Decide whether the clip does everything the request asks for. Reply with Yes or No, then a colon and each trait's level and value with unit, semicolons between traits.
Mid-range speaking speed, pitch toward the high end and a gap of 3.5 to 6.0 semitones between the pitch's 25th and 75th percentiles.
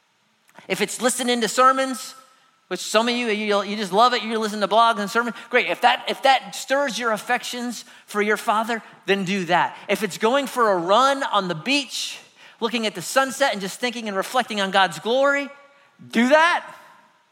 Yes: average, 195 wpm; high, 235 Hz; average, 4.1 semitones